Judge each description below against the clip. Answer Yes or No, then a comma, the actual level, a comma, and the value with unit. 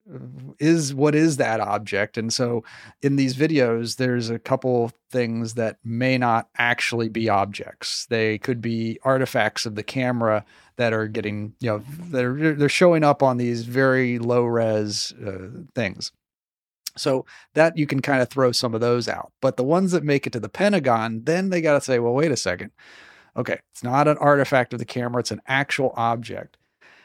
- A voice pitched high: No, low, 125 Hz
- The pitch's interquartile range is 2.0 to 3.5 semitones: Yes, average, 3.1 semitones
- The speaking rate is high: No, average, 185 wpm